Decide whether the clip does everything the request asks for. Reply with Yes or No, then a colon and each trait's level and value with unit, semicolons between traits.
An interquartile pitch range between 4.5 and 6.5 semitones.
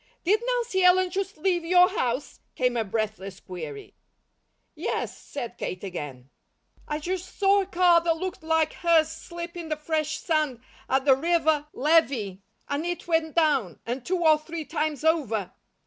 Yes: average, 5.3 semitones